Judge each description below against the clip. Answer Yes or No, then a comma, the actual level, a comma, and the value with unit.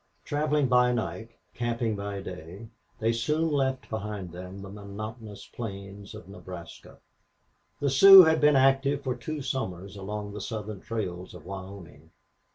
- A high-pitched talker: No, low, 110 Hz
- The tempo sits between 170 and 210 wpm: No, average, 145 wpm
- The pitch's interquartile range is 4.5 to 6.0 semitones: Yes, average, 5.2 semitones